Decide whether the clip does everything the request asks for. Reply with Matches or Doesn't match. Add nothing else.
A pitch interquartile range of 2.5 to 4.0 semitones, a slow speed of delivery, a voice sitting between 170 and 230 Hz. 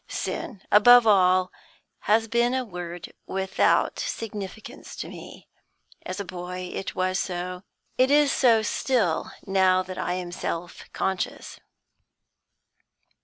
Matches